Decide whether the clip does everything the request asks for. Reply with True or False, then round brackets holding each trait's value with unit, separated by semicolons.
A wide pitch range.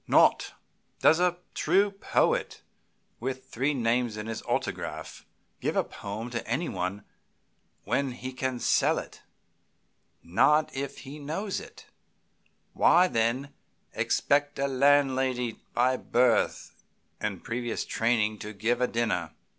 False (3.6 semitones)